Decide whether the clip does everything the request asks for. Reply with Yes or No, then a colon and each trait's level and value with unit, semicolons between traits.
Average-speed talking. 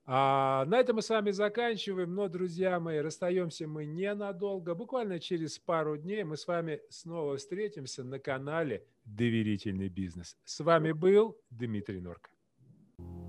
Yes: average, 140 wpm